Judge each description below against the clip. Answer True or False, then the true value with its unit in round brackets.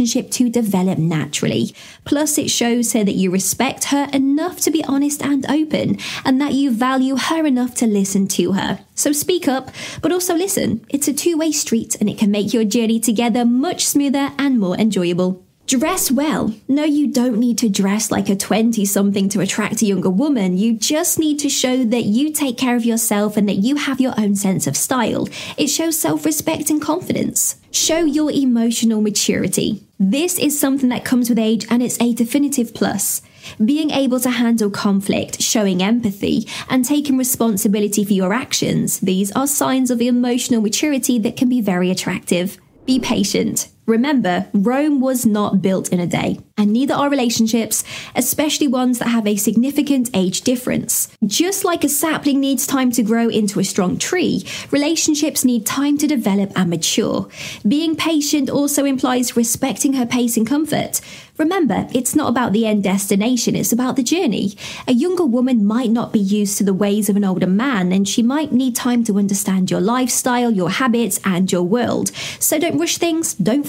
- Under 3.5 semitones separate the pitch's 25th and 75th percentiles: False (5.1 semitones)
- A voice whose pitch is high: True (245 Hz)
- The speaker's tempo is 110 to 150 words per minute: False (185 wpm)